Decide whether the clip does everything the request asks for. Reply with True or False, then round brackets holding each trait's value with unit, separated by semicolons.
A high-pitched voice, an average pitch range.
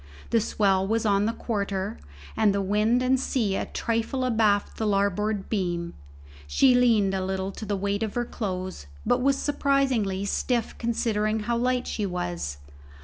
True (210 Hz; 3.3 semitones)